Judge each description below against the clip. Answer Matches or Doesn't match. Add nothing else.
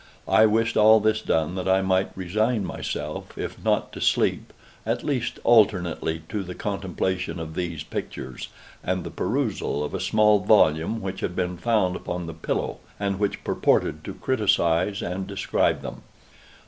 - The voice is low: Matches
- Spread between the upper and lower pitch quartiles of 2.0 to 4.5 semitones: Matches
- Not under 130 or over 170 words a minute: Matches